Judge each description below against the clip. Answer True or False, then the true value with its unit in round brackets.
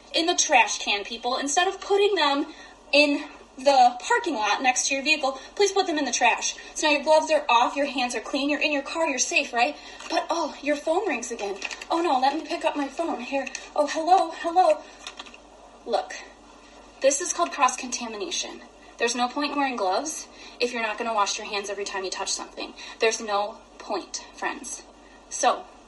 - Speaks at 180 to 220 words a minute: True (205 wpm)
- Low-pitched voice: False (285 Hz)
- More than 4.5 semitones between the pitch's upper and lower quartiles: True (5.3 semitones)